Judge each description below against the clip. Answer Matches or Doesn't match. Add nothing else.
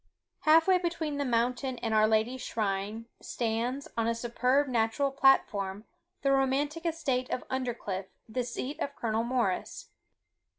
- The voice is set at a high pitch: Matches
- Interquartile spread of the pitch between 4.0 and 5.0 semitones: Doesn't match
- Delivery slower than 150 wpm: Matches